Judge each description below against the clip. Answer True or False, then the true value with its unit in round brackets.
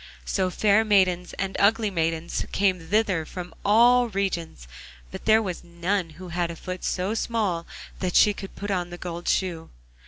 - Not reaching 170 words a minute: False (175 wpm)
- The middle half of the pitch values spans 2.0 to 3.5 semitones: True (2.9 semitones)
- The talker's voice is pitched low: False (185 Hz)